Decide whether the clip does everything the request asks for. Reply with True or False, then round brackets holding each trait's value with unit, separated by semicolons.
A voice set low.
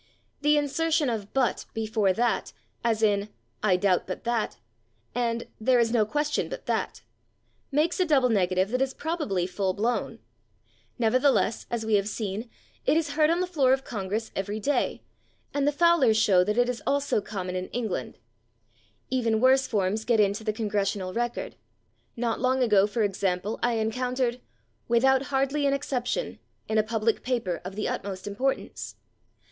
False (230 Hz)